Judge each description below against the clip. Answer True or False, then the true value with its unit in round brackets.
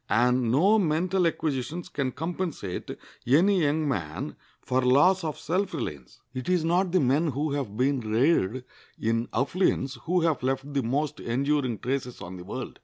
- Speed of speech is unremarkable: True (165 wpm)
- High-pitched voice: False (140 Hz)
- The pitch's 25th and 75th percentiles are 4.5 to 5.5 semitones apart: True (5.0 semitones)